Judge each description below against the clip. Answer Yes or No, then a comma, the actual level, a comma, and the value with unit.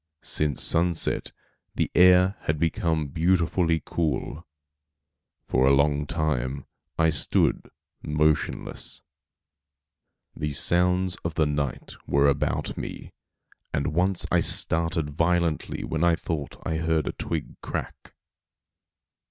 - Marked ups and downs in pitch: No, average, 2.7 semitones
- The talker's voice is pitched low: Yes, very low, 80 Hz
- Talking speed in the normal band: No, slow, 110 wpm